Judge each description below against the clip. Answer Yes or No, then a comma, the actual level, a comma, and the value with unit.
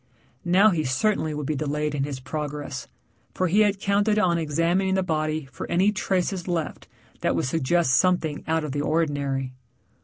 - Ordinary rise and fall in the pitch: Yes, average, 4.0 semitones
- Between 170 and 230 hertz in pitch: No, medium, 160 Hz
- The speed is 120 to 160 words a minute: No, average, 175 wpm